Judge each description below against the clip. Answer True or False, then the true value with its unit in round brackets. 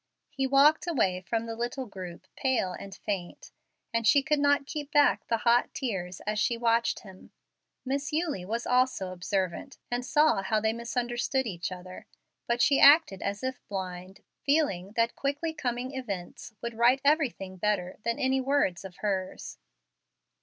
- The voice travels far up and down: True (5.8 semitones)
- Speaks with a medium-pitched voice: False (235 Hz)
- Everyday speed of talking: True (160 wpm)